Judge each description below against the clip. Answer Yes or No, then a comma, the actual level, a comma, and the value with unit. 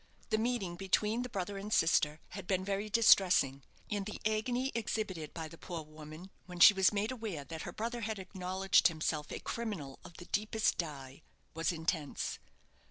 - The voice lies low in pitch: No, high, 190 Hz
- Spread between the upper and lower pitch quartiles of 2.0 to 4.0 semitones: No, average, 4.9 semitones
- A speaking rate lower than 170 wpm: No, average, 175 wpm